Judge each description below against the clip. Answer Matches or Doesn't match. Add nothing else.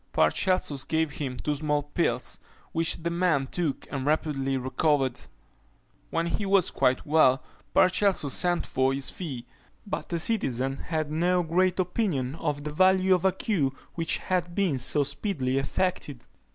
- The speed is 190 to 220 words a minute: Doesn't match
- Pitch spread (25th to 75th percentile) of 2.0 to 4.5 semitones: Doesn't match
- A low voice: Doesn't match